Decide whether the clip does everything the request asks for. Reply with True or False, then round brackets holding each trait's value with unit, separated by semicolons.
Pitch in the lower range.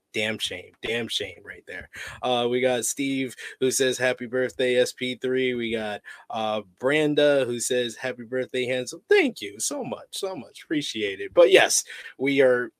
True (130 Hz)